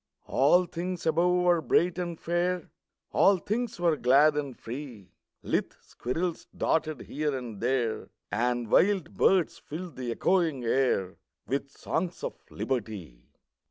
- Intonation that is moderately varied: No, wide, 6.1 semitones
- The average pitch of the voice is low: No, medium, 155 Hz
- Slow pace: Yes, slow, 130 wpm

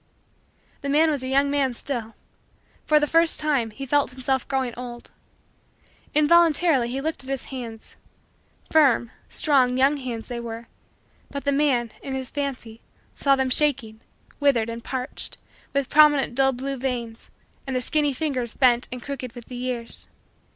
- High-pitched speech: Yes, very high, 265 Hz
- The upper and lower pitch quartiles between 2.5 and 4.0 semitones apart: Yes, average, 2.8 semitones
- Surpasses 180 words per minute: No, average, 160 wpm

